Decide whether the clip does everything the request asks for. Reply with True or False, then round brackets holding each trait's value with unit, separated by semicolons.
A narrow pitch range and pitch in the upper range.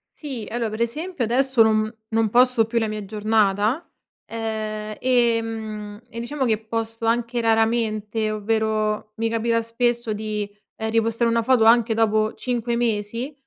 True (1.5 semitones; 225 Hz)